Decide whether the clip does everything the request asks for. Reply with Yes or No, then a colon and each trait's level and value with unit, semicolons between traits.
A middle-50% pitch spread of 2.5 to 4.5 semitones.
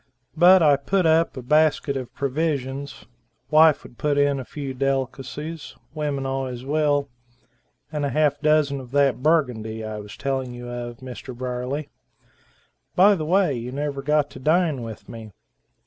Yes: average, 3.2 semitones